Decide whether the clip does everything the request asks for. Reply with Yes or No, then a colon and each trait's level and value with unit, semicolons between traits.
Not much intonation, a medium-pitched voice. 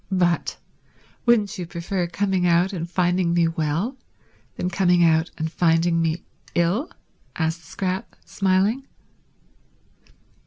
Yes: narrow, 2.2 semitones; medium, 175 Hz